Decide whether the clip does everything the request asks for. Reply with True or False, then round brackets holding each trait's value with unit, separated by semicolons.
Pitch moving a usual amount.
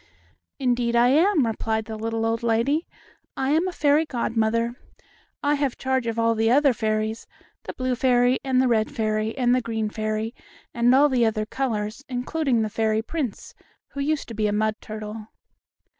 True (3.1 semitones)